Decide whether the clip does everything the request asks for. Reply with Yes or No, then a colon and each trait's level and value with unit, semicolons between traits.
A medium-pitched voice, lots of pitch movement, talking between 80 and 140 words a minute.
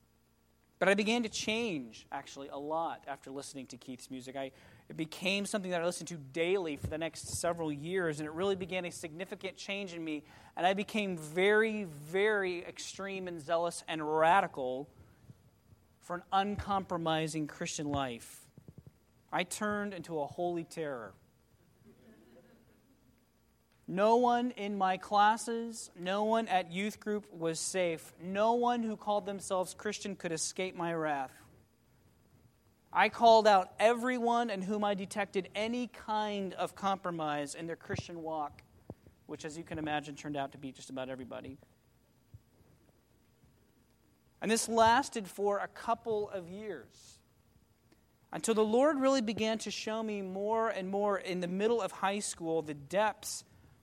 No: medium, 175 Hz; wide, 6.0 semitones; average, 150 wpm